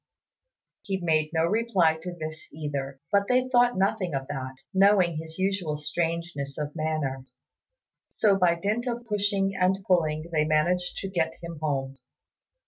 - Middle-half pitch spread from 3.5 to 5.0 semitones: Yes, average, 4.1 semitones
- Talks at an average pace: Yes, average, 150 wpm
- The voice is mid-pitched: Yes, medium, 170 Hz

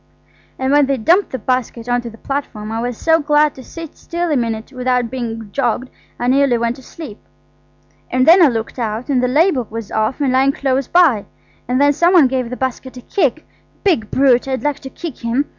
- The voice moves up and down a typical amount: Yes, average, 3.3 semitones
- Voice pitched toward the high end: Yes, very high, 260 Hz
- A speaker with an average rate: No, fast, 215 wpm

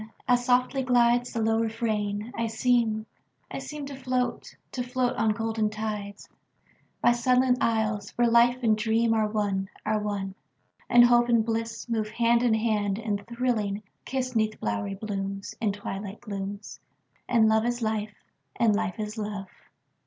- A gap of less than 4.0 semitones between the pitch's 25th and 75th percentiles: Yes, narrow, 2.4 semitones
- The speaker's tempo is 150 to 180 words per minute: No, slow, 135 wpm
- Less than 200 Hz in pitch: No, high, 220 Hz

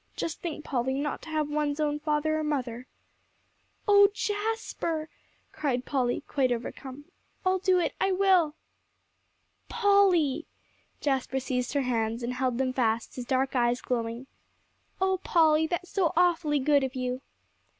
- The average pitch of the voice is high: Yes, very high, 290 Hz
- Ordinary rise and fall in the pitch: Yes, average, 4.8 semitones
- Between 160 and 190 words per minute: No, average, 145 wpm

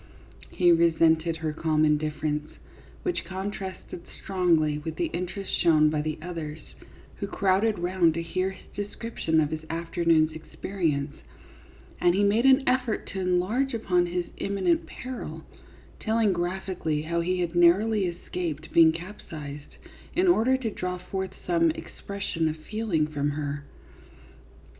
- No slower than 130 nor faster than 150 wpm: Yes, average, 140 wpm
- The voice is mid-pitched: Yes, medium, 175 Hz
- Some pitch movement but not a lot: Yes, average, 3.7 semitones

